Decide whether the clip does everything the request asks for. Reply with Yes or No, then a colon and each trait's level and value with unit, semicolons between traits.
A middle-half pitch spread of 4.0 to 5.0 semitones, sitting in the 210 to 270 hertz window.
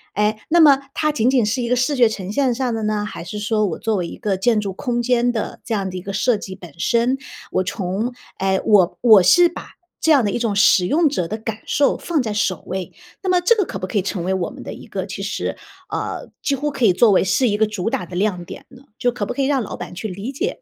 Yes: average, 4.6 semitones; high, 215 Hz